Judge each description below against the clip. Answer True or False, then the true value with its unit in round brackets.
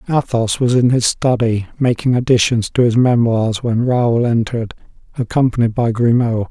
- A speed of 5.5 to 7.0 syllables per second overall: False (4.9 syllables/s)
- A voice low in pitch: True (120 Hz)